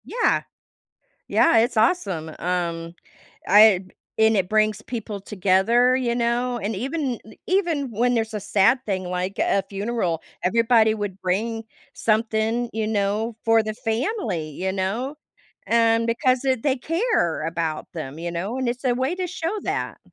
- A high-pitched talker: Yes, high, 220 Hz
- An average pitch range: Yes, average, 4.2 semitones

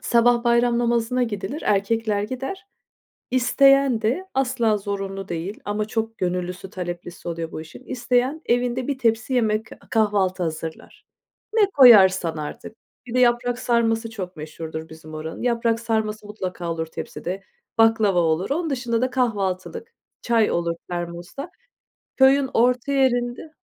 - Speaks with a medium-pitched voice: No, high, 225 Hz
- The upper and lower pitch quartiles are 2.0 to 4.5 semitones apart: No, average, 4.9 semitones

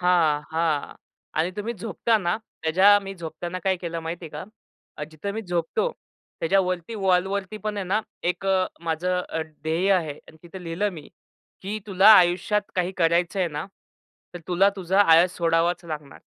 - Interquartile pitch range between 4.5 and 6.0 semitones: No, average, 2.8 semitones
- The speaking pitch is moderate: Yes, medium, 180 Hz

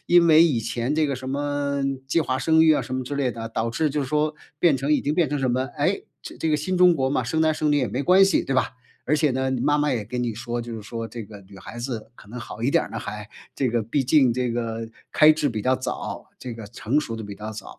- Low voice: Yes, low, 130 Hz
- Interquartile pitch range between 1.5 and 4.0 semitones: No, average, 4.4 semitones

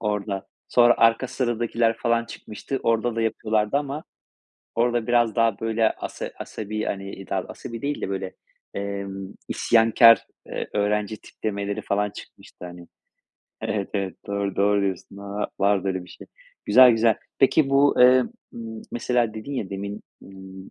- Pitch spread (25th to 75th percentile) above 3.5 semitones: No, average, 2.8 semitones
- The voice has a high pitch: No, low, 110 Hz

